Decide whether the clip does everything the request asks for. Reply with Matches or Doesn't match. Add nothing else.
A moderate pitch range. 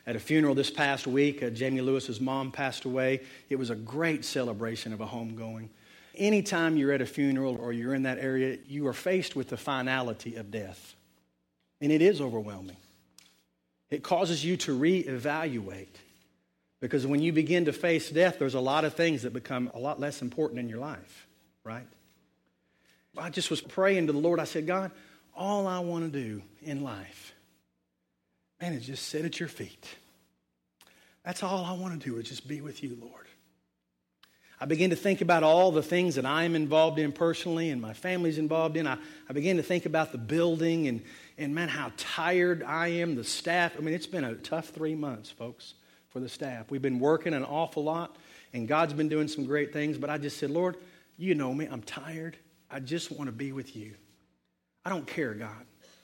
Doesn't match